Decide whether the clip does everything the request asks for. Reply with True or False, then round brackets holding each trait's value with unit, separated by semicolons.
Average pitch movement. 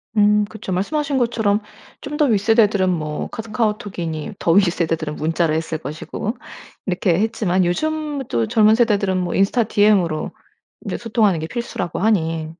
True (4.9 semitones)